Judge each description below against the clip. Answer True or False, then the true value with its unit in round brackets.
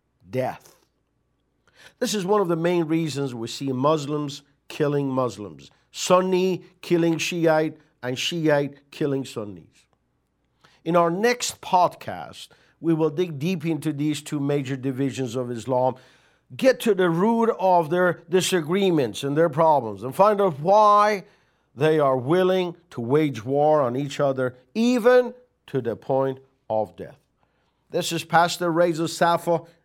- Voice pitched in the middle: True (160 Hz)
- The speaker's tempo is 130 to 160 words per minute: True (140 wpm)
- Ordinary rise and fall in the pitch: True (4.7 semitones)